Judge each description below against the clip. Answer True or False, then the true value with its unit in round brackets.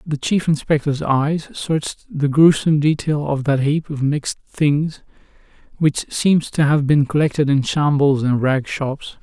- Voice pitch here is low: False (145 Hz)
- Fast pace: False (165 wpm)